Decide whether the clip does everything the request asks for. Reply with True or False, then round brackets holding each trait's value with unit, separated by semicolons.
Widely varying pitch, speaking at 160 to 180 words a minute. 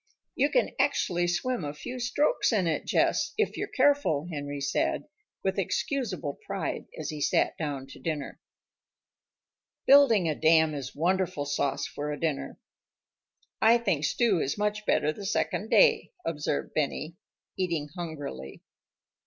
False (7.6 semitones; 145 wpm)